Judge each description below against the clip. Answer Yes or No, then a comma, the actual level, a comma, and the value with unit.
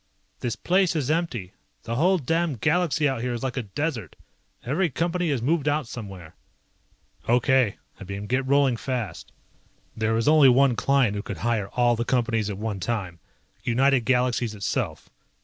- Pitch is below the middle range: Yes, low, 125 Hz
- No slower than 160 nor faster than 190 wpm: Yes, average, 165 wpm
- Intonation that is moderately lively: Yes, average, 4.4 semitones